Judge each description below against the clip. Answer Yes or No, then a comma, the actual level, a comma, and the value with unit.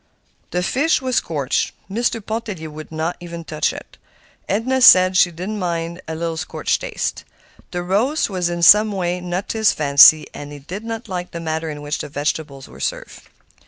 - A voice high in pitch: No, medium, 175 Hz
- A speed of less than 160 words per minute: No, average, 190 wpm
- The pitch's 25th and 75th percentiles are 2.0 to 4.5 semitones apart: No, average, 5.1 semitones